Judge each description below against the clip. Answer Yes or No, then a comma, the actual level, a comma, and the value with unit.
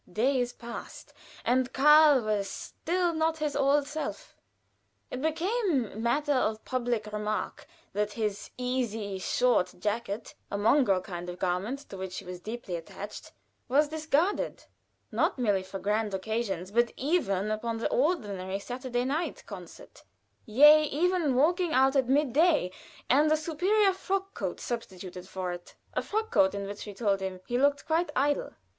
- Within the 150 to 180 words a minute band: Yes, average, 155 wpm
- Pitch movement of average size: No, wide, 6.7 semitones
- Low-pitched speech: No, high, 245 Hz